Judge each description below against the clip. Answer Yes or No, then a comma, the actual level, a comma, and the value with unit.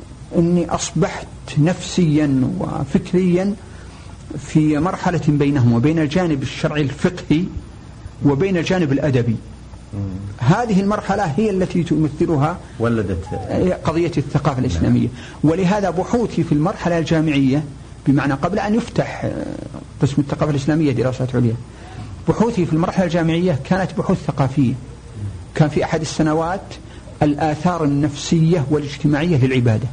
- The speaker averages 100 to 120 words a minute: Yes, average, 105 wpm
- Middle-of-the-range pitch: Yes, medium, 150 Hz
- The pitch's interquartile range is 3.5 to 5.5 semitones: Yes, average, 5.0 semitones